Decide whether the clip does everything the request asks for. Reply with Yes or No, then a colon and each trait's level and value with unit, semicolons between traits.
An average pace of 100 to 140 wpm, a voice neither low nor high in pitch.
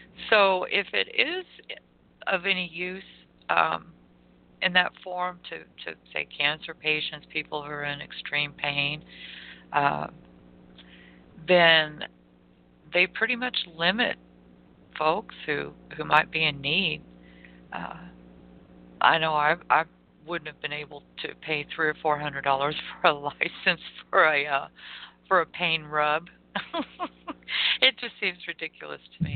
Yes: slow, 135 wpm; medium, 150 Hz